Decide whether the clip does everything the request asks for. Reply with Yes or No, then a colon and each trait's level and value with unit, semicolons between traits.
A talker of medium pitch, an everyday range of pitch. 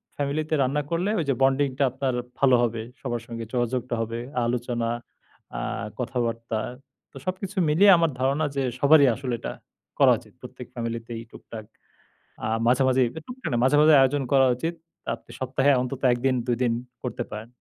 No: low, 130 Hz; average, 3.3 semitones